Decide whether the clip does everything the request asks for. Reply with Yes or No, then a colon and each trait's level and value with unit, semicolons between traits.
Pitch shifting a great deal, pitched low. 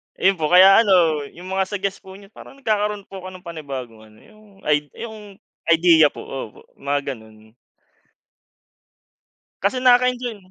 No: wide, 5.9 semitones; medium, 185 Hz